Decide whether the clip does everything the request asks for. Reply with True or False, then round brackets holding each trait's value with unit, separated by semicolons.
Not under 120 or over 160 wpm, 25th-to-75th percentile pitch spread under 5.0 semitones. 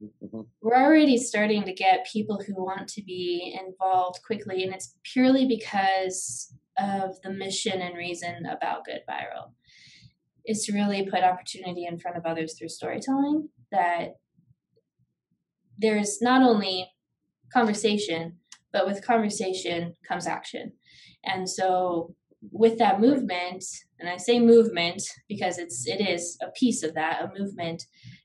True (135 wpm; 3.8 semitones)